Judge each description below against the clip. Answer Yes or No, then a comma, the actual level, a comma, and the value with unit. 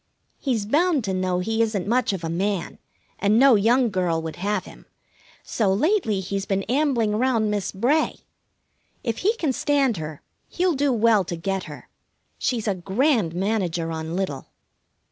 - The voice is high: Yes, high, 210 Hz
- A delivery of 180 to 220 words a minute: No, average, 165 wpm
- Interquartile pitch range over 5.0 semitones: Yes, wide, 5.4 semitones